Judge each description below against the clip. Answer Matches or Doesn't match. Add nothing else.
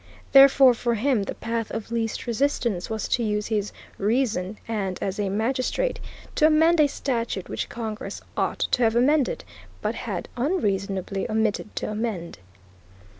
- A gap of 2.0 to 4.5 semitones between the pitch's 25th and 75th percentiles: Matches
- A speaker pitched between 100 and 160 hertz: Doesn't match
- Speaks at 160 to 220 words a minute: Doesn't match